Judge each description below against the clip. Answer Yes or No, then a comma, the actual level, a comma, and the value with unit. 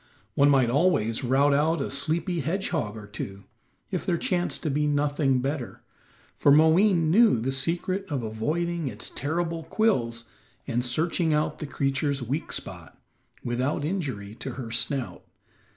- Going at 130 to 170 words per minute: Yes, average, 150 wpm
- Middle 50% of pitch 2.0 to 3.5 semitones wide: No, average, 4.8 semitones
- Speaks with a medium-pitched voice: Yes, medium, 145 Hz